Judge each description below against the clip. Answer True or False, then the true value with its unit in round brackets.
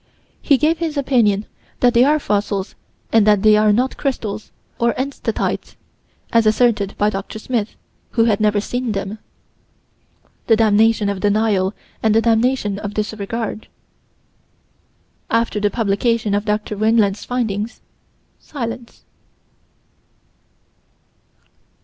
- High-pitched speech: True (220 Hz)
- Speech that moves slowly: True (120 wpm)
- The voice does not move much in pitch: True (2.3 semitones)